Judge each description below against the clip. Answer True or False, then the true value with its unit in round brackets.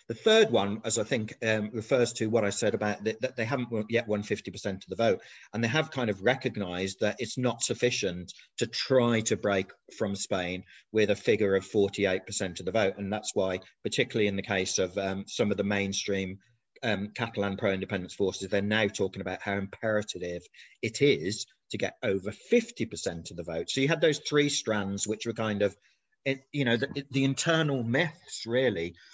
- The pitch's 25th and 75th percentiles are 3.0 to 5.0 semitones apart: True (3.6 semitones)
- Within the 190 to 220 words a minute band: True (200 wpm)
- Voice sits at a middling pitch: False (105 Hz)